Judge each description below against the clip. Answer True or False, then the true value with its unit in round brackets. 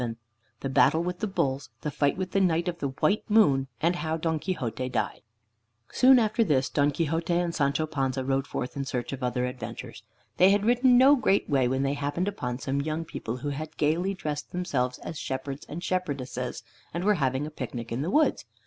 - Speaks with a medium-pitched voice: True (150 Hz)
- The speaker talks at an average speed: False (210 wpm)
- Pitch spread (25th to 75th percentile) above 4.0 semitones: True (5.1 semitones)